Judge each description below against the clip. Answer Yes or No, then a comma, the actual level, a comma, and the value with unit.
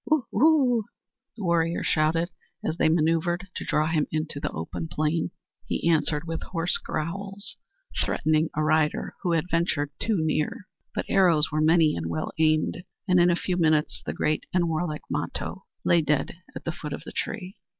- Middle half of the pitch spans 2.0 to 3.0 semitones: Yes, narrow, 2.4 semitones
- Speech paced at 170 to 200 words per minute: Yes, average, 180 wpm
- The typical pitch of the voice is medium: Yes, medium, 165 Hz